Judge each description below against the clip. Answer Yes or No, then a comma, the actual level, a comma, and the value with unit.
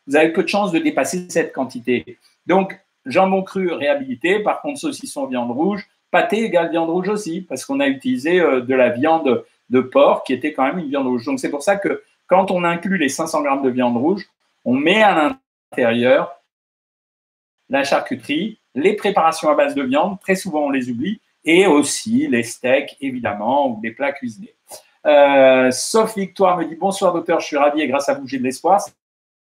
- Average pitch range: No, wide, 8.5 semitones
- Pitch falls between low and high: Yes, medium, 180 Hz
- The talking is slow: No, average, 195 wpm